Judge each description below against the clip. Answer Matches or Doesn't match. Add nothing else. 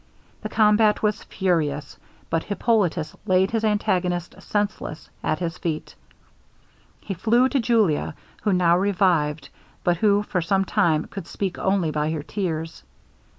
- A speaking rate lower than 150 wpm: Matches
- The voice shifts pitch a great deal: Doesn't match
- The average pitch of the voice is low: Doesn't match